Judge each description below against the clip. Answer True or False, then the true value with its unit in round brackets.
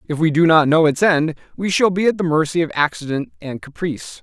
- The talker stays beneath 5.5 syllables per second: False (5.7 syllables/s)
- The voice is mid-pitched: True (160 Hz)